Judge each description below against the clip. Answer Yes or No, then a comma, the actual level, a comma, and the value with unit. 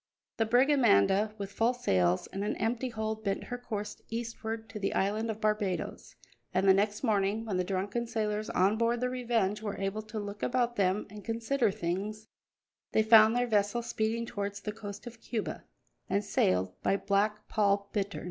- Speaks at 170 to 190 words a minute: Yes, average, 185 wpm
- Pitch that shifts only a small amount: Yes, narrow, 2.2 semitones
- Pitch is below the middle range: No, high, 215 Hz